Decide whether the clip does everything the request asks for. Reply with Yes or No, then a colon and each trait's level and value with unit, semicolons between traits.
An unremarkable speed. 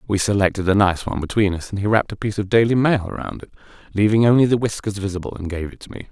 No: fast, 265 wpm